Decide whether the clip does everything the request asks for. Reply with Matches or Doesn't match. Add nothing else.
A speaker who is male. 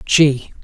Matches